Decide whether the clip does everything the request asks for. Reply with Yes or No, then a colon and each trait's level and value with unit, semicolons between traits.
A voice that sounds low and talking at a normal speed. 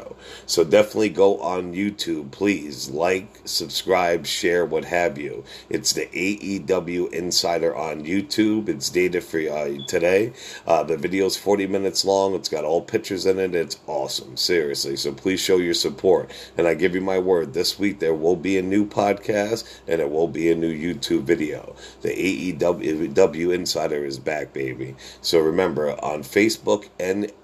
Yes: very low, 95 Hz; average, 170 wpm